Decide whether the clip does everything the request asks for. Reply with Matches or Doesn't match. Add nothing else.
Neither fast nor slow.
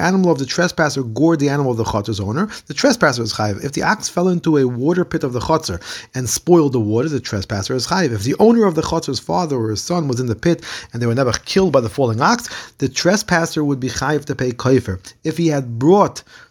Doesn't match